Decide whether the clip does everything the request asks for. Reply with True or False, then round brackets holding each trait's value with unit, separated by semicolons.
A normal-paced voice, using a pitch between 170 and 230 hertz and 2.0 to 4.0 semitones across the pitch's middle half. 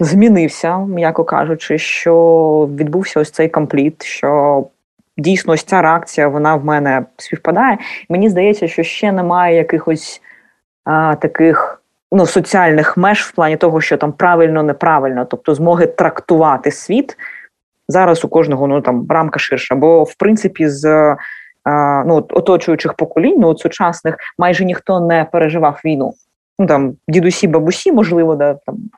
False (145 wpm; 160 Hz; 2.5 semitones)